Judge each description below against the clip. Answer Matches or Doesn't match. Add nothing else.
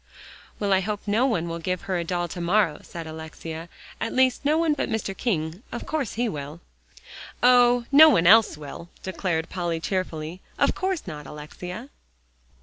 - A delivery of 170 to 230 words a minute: Matches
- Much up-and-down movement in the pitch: Matches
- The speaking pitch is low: Doesn't match